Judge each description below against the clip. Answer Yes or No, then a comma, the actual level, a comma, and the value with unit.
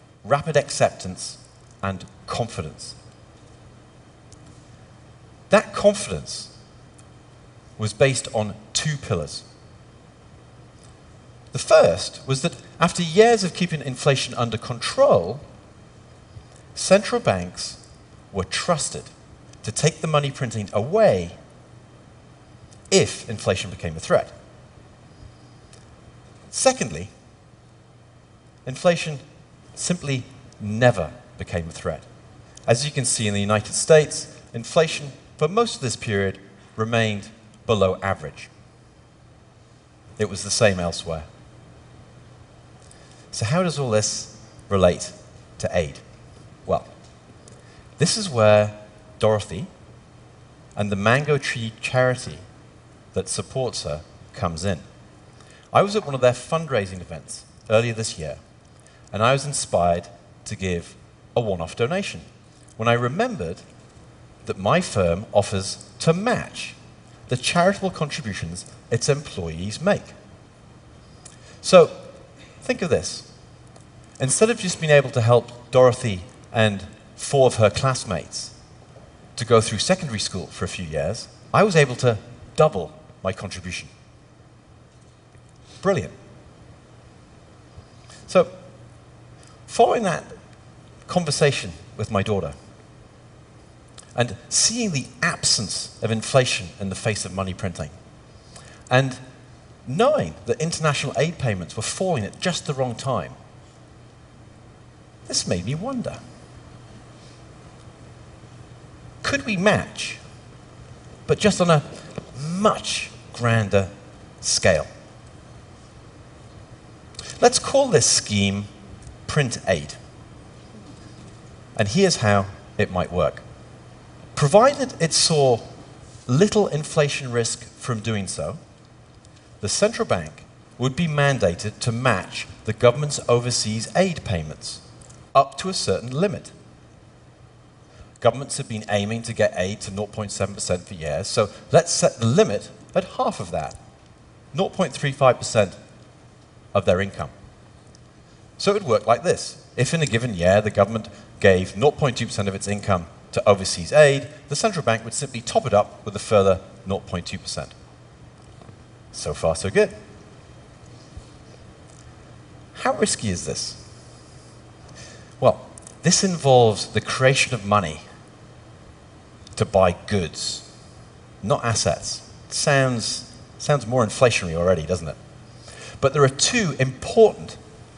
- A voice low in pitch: Yes, low, 120 Hz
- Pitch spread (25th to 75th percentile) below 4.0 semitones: No, average, 5.2 semitones